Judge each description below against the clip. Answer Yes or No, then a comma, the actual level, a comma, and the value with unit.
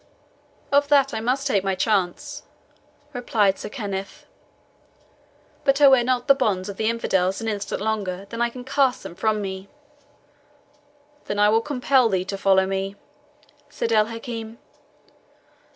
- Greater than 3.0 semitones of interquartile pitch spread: Yes, average, 4.4 semitones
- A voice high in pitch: Yes, high, 220 Hz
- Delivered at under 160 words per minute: Yes, average, 150 wpm